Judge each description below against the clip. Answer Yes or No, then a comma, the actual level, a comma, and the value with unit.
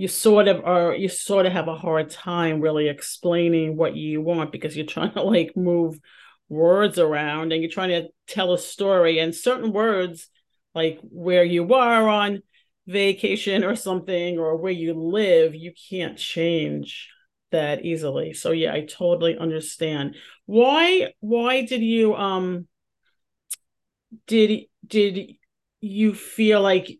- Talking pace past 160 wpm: No, average, 145 wpm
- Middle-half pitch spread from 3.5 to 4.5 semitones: Yes, average, 4.0 semitones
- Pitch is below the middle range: No, medium, 180 Hz